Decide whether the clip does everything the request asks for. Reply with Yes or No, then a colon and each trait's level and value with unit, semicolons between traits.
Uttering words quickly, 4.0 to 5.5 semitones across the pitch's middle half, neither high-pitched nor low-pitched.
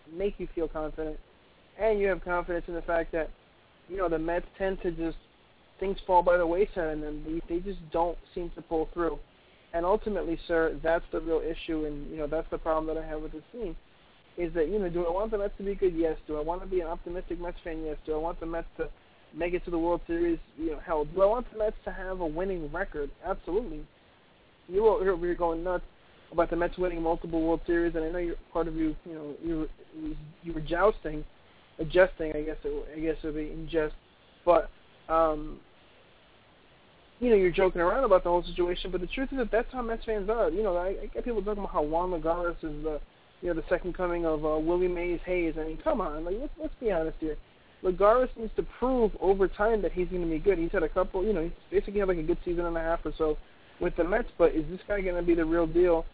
No: fast, 250 wpm; average, 2.7 semitones; medium, 170 Hz